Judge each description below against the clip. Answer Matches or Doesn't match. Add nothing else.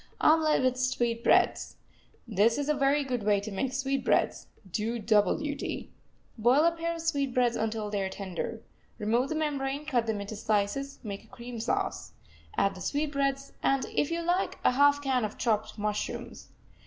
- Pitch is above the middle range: Matches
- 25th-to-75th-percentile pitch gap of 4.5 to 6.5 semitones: Matches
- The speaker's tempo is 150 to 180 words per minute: Matches